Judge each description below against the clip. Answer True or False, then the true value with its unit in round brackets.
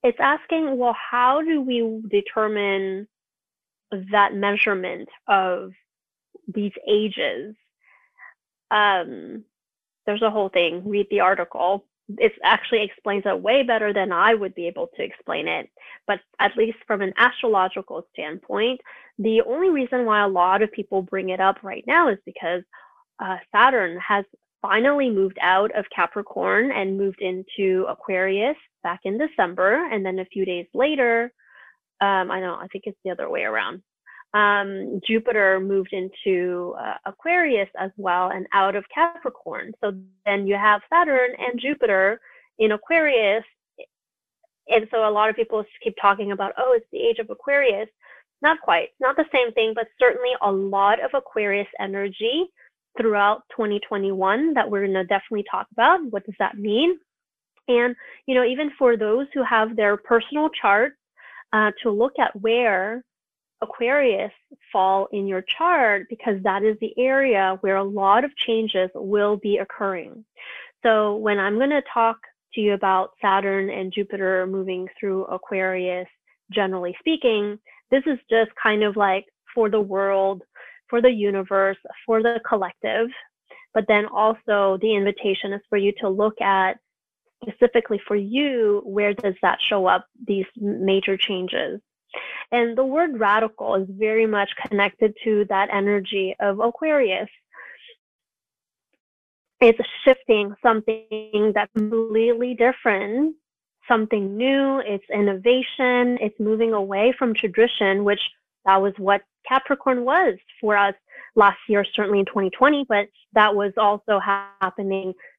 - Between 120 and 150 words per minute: True (145 wpm)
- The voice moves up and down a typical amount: True (3.6 semitones)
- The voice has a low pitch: False (210 Hz)